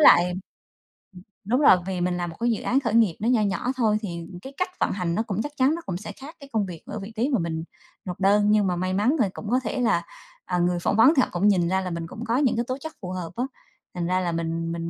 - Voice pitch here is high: Yes, high, 200 Hz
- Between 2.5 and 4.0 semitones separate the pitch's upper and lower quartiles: No, average, 5.0 semitones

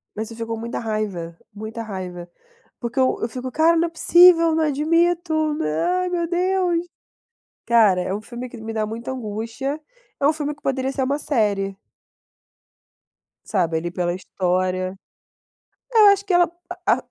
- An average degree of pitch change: No, wide, 8.0 semitones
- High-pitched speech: Yes, high, 235 Hz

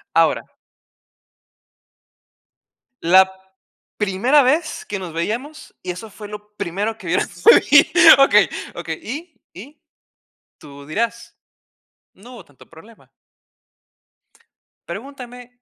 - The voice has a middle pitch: No, high, 220 Hz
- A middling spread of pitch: No, wide, 5.7 semitones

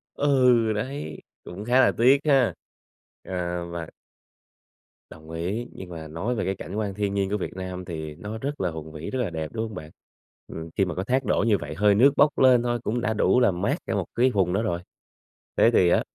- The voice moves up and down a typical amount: No, wide, 5.7 semitones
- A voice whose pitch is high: No, low, 100 Hz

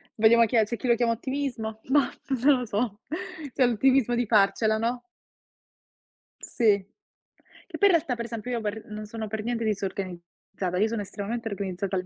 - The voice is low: No, high, 225 Hz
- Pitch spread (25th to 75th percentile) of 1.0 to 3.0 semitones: Yes, average, 2.7 semitones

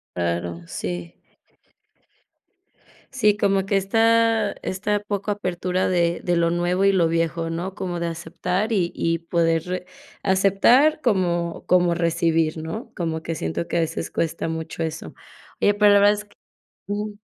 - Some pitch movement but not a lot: Yes, average, 3.5 semitones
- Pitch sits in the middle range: Yes, medium, 175 Hz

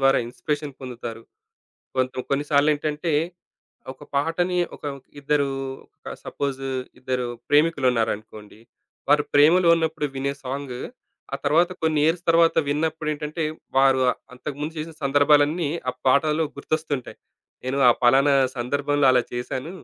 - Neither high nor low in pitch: Yes, medium, 145 Hz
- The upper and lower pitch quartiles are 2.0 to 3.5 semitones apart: Yes, average, 2.9 semitones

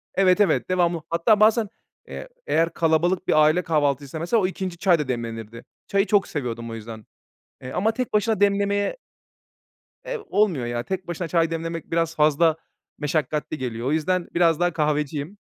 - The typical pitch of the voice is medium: Yes, medium, 165 Hz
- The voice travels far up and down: No, average, 4.3 semitones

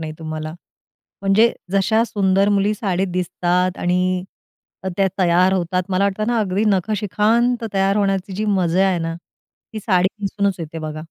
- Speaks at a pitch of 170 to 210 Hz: Yes, high, 190 Hz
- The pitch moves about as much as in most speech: No, narrow, 2.3 semitones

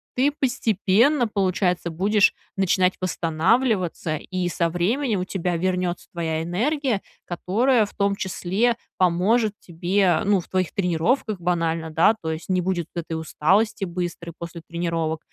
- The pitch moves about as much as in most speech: Yes, average, 3.6 semitones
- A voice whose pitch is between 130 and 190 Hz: Yes, medium, 185 Hz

